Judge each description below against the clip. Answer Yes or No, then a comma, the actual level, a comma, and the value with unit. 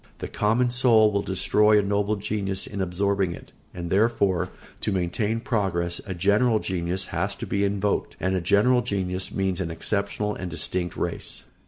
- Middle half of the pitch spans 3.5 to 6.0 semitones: No, narrow, 2.4 semitones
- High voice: No, low, 100 Hz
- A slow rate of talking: No, average, 170 wpm